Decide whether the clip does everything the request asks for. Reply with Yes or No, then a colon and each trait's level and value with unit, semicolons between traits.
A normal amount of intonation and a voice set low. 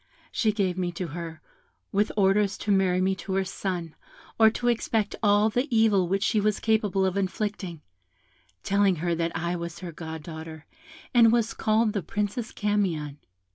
No: average, 3.5 semitones; high, 195 Hz